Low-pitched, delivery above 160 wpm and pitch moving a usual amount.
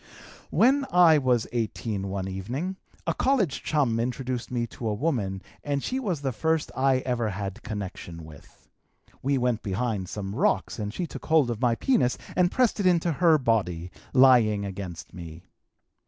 No: low, 125 Hz; average, 170 wpm; wide, 7.4 semitones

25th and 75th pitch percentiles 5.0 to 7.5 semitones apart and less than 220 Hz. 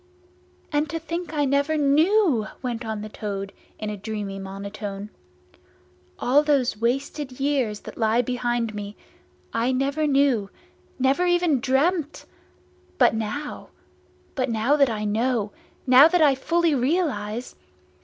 No: average, 5.3 semitones; very high, 255 Hz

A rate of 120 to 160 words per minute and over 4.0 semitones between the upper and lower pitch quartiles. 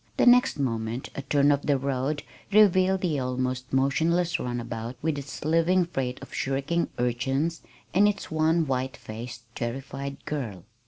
Yes: average, 150 wpm; average, 4.6 semitones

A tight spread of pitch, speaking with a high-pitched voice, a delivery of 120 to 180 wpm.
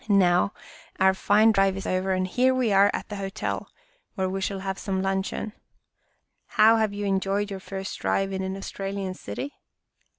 Yes: narrow, 1.2 semitones; high, 195 Hz; average, 175 wpm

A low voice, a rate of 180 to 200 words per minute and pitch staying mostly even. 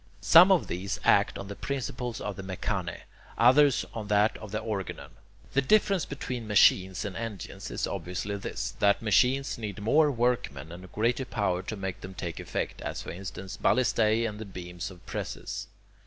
No: low, 105 Hz; average, 185 wpm; average, 4.4 semitones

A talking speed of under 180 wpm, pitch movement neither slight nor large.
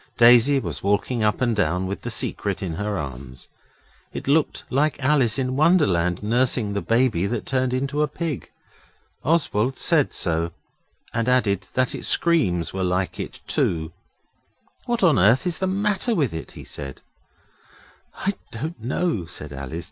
No: average, 160 wpm; wide, 7.7 semitones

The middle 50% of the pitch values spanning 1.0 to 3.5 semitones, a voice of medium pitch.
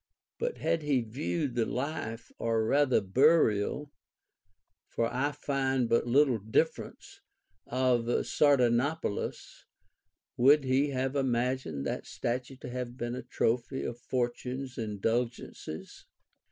No: average, 2.8 semitones; low, 125 Hz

